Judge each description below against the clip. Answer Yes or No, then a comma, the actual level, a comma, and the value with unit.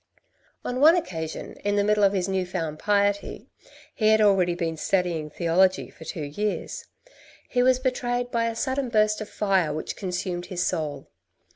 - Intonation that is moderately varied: Yes, average, 3.9 semitones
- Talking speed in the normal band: Yes, average, 170 wpm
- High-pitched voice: Yes, high, 195 Hz